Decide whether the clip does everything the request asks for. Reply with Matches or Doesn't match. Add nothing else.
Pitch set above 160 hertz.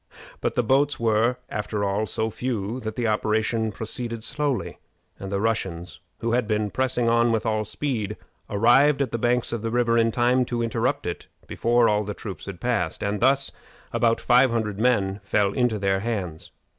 Doesn't match